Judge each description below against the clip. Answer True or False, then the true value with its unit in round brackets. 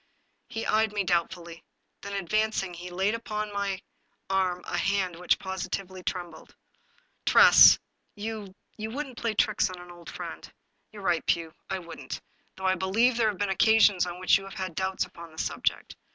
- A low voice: False (190 Hz)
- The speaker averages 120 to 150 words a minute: False (190 wpm)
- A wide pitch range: False (3.0 semitones)